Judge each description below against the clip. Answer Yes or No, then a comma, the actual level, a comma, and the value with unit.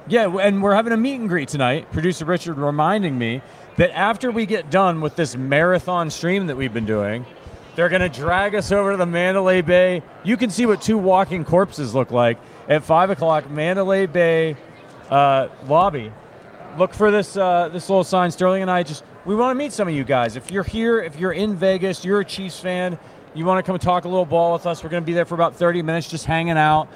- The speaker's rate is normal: No, fast, 225 wpm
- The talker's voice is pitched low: No, medium, 180 Hz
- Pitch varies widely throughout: No, average, 3.7 semitones